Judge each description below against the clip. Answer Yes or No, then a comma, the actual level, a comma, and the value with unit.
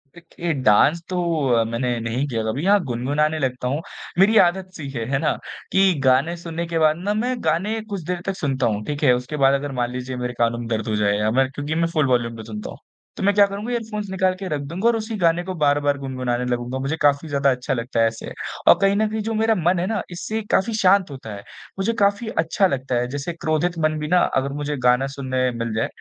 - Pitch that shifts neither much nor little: No, wide, 6.7 semitones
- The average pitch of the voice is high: No, medium, 145 Hz